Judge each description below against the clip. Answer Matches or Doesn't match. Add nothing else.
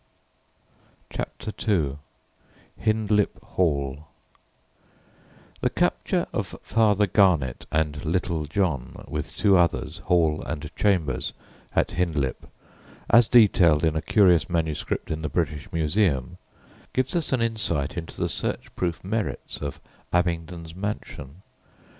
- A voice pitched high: Doesn't match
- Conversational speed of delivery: Doesn't match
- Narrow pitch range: Doesn't match